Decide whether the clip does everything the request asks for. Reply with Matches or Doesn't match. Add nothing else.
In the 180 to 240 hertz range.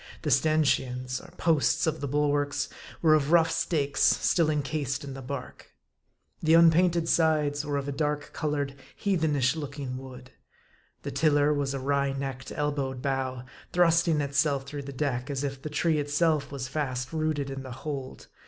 Doesn't match